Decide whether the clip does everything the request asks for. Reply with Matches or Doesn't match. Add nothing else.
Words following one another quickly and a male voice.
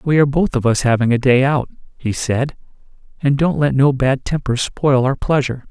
Matches